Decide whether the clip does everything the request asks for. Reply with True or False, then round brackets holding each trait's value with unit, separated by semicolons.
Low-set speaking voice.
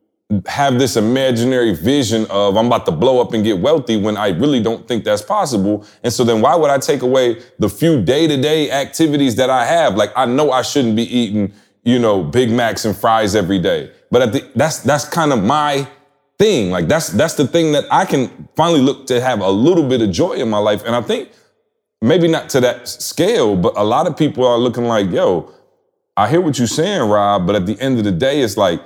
True (125 Hz)